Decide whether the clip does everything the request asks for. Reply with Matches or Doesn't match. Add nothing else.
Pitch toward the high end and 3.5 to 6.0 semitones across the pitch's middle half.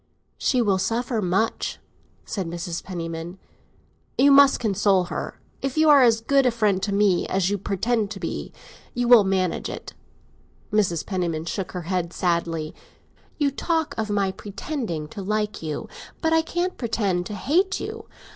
Matches